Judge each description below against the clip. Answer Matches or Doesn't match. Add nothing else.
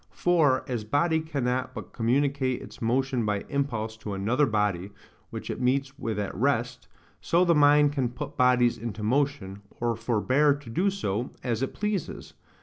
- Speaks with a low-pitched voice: Matches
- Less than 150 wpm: Doesn't match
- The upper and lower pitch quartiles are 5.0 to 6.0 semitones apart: Doesn't match